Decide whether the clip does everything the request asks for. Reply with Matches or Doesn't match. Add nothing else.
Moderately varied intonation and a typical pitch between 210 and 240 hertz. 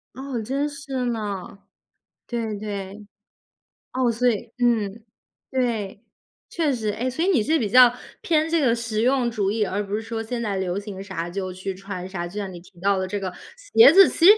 Matches